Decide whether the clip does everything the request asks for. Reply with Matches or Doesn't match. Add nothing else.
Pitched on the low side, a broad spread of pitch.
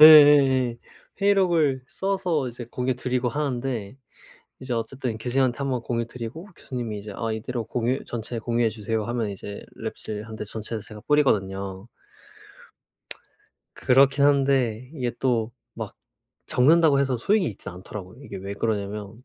Doesn't match